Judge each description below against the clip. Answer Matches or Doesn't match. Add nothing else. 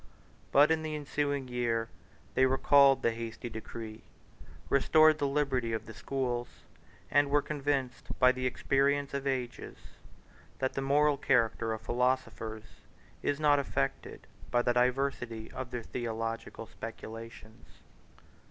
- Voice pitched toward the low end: Matches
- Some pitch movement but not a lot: Matches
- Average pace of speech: Doesn't match